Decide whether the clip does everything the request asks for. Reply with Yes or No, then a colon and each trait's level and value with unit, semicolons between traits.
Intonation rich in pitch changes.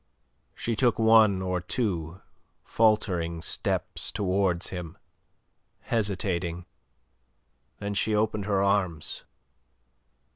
No: average, 3.3 semitones